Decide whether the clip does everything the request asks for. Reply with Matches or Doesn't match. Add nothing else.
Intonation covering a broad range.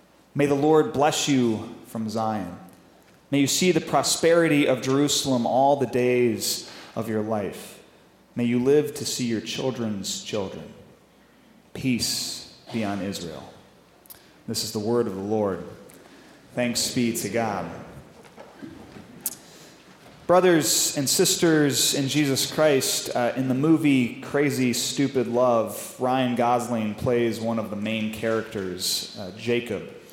Doesn't match